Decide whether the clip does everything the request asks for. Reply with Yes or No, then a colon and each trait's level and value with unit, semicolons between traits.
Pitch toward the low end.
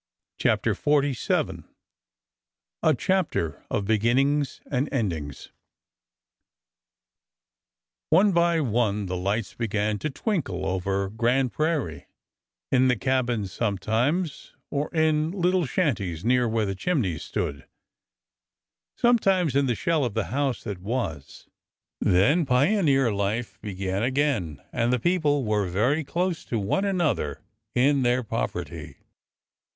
Yes: low, 125 Hz